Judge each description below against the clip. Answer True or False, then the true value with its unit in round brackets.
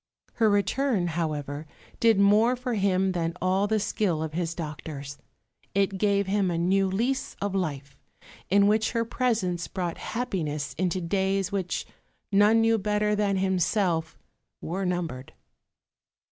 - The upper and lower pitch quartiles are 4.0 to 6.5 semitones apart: False (3.6 semitones)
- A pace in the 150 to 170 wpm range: False (140 wpm)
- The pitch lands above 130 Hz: True (190 Hz)